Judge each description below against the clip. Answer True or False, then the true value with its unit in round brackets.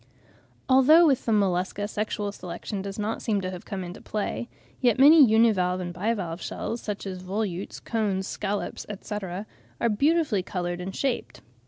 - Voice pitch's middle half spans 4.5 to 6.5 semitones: False (3.6 semitones)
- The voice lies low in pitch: False (205 Hz)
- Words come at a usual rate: True (160 wpm)